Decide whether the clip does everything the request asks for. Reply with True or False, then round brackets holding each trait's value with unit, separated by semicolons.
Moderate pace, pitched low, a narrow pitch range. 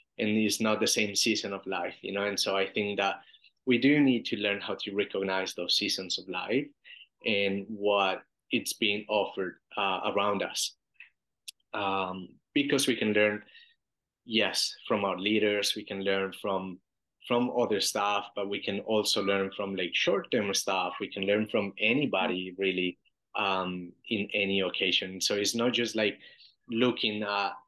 True (165 wpm; 100 Hz; 1.9 semitones)